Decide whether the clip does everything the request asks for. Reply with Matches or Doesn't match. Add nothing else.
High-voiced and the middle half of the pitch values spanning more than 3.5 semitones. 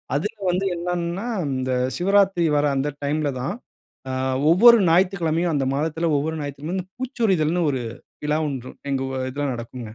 Doesn't match